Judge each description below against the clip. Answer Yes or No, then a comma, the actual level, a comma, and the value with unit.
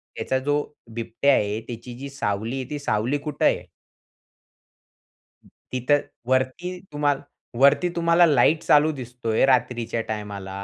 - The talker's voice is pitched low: Yes, low, 130 Hz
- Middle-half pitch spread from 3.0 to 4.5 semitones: Yes, average, 4.1 semitones